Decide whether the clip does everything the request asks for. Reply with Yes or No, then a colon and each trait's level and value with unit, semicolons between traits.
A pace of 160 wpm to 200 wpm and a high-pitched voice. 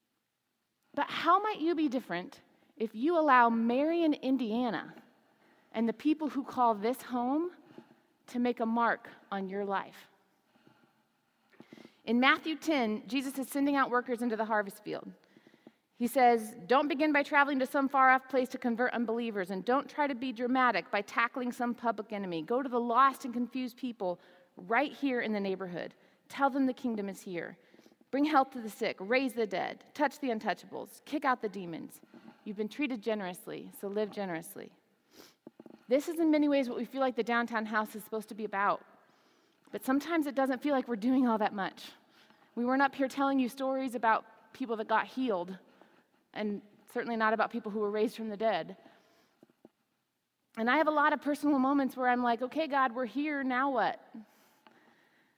Yes: average, 185 wpm; high, 245 Hz